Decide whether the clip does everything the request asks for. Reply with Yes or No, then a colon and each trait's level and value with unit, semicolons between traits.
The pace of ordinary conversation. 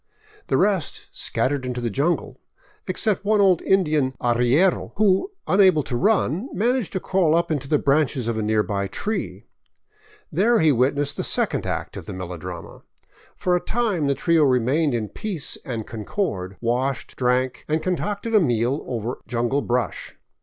Yes: average, 160 wpm